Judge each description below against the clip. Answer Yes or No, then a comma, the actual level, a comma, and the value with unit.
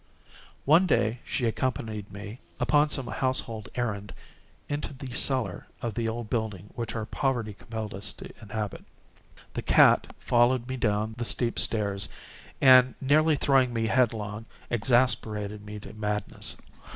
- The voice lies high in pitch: No, low, 115 Hz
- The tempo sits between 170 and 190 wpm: No, average, 140 wpm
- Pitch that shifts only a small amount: No, average, 3.4 semitones